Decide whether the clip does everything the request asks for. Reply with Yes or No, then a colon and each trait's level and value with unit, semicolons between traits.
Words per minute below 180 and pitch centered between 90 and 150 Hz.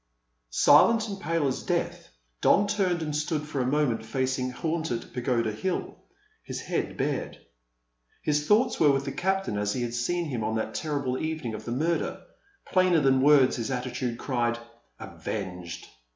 Yes: average, 165 wpm; low, 135 Hz